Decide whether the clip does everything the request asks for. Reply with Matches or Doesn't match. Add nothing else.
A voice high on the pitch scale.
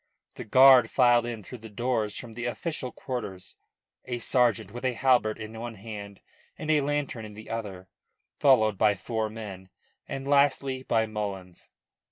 Doesn't match